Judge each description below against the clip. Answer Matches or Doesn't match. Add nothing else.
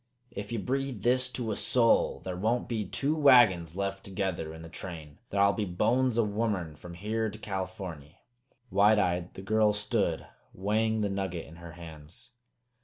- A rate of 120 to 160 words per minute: Doesn't match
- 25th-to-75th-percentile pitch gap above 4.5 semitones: Doesn't match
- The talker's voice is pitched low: Matches